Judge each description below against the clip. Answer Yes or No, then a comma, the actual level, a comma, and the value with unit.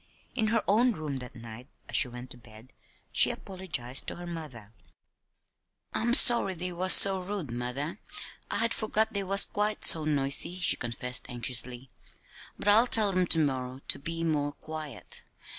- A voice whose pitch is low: No, medium, 155 Hz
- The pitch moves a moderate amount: No, wide, 7.8 semitones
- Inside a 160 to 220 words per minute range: Yes, average, 170 wpm